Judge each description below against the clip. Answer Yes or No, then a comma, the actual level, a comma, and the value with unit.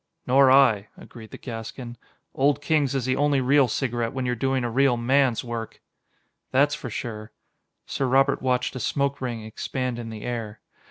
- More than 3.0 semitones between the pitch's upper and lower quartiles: No, narrow, 2.6 semitones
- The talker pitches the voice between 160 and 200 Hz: No, low, 125 Hz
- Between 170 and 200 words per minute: Yes, average, 175 wpm